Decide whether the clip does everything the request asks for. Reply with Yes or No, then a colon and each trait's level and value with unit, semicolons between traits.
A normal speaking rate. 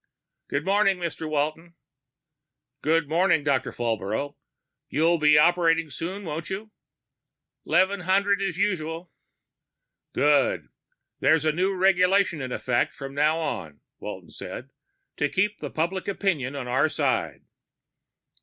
No: slow, 115 wpm